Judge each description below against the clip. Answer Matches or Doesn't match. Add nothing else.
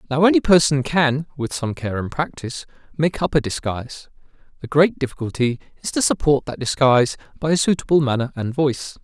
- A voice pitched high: Doesn't match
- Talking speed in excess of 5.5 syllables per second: Matches